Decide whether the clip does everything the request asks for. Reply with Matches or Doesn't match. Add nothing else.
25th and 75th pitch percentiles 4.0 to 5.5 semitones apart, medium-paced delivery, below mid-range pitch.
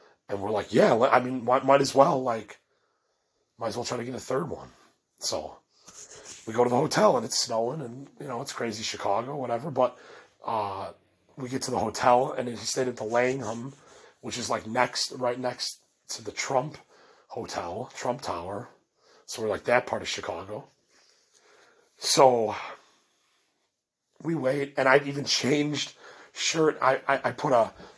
Doesn't match